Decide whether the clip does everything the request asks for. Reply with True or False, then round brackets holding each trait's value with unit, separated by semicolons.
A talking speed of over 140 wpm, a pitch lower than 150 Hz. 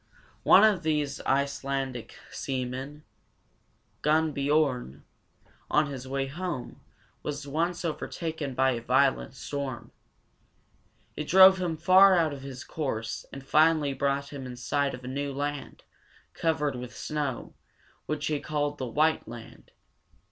False (135 wpm; 140 Hz)